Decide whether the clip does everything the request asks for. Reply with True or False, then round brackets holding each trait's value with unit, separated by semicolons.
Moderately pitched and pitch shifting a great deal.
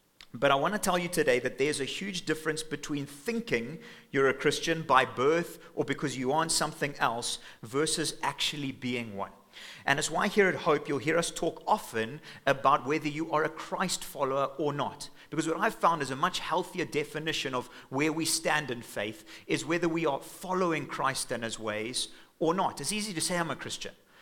False (150 Hz; 3.5 semitones)